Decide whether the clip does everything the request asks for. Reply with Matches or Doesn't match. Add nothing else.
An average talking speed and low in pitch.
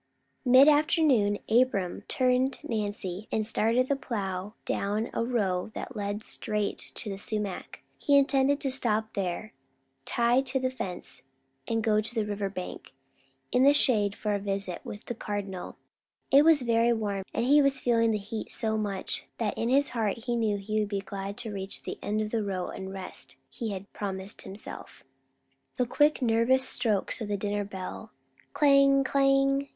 Doesn't match